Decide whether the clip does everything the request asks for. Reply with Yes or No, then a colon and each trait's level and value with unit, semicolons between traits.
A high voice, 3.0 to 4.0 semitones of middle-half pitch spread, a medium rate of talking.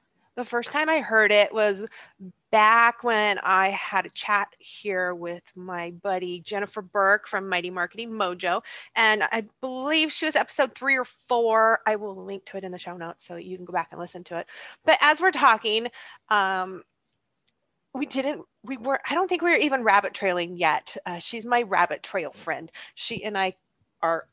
No: high, 210 Hz; average, 4.7 semitones; average, 190 wpm